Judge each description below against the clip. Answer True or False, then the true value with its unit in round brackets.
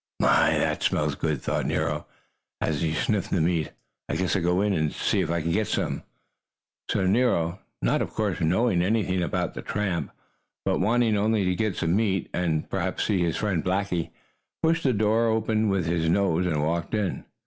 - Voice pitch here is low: True (95 Hz)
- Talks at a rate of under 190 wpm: False (195 wpm)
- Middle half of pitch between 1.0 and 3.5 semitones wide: False (4.1 semitones)